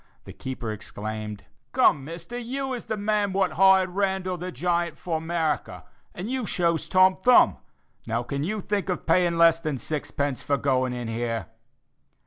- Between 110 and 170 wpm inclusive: Yes, average, 165 wpm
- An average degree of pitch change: No, wide, 5.7 semitones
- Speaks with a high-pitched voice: No, medium, 170 Hz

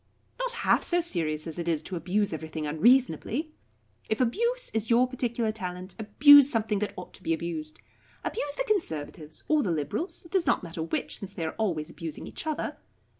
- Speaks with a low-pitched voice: No, high, 205 Hz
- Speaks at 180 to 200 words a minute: Yes, average, 190 wpm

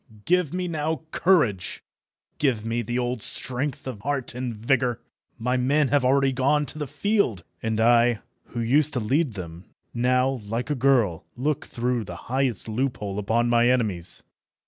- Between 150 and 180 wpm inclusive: Yes, average, 165 wpm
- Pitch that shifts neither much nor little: Yes, average, 3.5 semitones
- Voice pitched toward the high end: No, low, 125 Hz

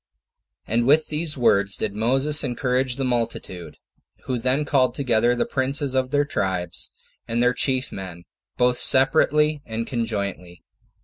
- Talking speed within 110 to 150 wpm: Yes, average, 145 wpm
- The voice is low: Yes, low, 125 Hz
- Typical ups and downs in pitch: Yes, average, 3.3 semitones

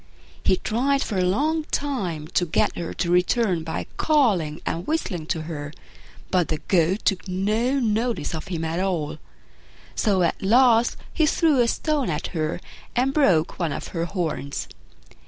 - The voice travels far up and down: Yes, wide, 6.7 semitones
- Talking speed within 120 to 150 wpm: No, average, 165 wpm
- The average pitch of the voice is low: No, high, 190 Hz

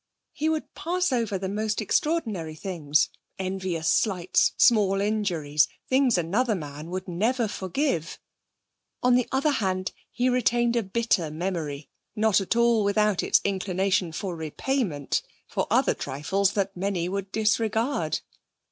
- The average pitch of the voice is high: Yes, high, 195 Hz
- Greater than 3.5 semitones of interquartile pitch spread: Yes, average, 4.9 semitones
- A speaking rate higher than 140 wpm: No, slow, 135 wpm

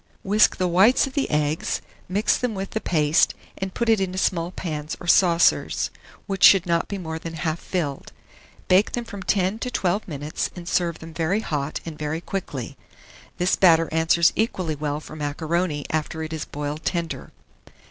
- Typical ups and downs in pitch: Yes, average, 3.6 semitones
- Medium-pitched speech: Yes, medium, 170 Hz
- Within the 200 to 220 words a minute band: No, average, 180 wpm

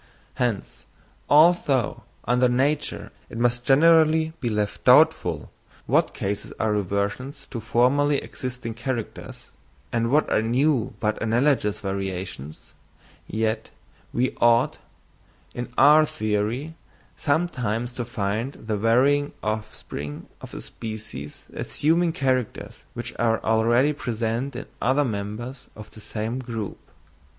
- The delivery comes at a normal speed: No, slow, 115 wpm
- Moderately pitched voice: No, low, 120 Hz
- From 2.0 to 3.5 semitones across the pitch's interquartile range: No, average, 3.9 semitones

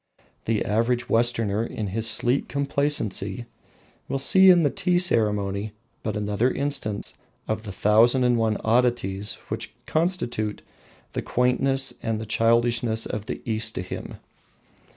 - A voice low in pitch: Yes, low, 115 Hz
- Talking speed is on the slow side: Yes, slow, 130 wpm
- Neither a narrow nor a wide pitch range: Yes, average, 3.0 semitones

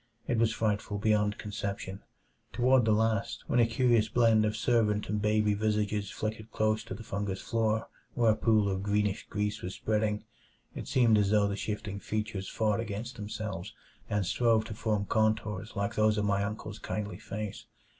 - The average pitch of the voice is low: Yes, low, 105 Hz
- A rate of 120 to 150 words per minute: No, average, 175 wpm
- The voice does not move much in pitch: Yes, narrow, 1.3 semitones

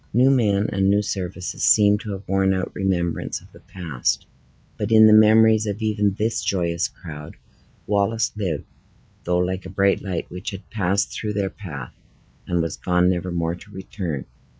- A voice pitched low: Yes, very low, 95 Hz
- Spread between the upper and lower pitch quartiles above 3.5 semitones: No, average, 2.8 semitones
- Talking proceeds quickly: No, average, 175 wpm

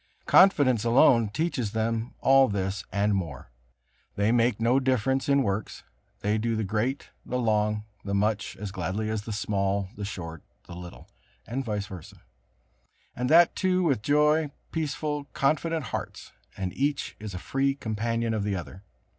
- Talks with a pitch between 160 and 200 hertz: No, low, 110 Hz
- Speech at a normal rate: Yes, average, 160 wpm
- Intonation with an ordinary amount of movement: Yes, average, 5.0 semitones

